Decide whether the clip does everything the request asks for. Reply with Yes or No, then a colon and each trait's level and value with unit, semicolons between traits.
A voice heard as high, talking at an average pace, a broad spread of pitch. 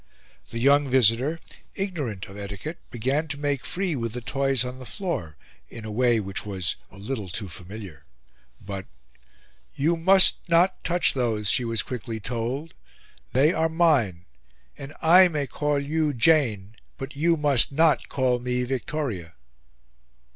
No: low, 130 Hz; average, 150 wpm; wide, 5.7 semitones